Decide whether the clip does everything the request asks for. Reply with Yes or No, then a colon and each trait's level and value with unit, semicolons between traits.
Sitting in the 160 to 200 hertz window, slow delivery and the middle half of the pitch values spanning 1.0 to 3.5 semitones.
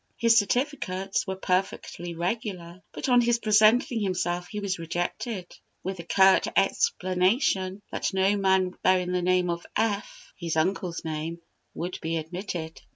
No: medium, 185 Hz; average, 145 wpm; average, 2.8 semitones